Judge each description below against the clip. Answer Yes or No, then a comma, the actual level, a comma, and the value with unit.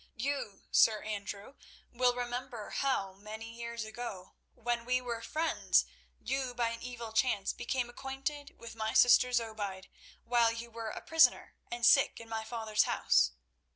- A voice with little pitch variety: Yes, narrow, 2.2 semitones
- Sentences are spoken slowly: No, average, 155 wpm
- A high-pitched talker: Yes, high, 235 Hz